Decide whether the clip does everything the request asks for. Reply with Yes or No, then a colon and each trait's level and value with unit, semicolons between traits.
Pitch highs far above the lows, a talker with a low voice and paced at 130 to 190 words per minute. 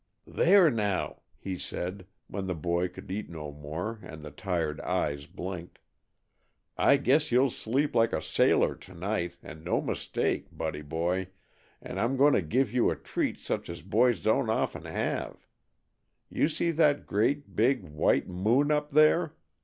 Yes: wide, 7.5 semitones; very low, 95 Hz; average, 165 wpm